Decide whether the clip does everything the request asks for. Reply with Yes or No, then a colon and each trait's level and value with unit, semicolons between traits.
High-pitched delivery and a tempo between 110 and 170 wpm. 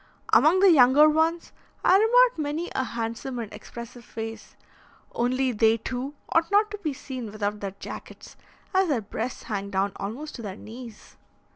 Yes: very high, 250 Hz; average, 165 wpm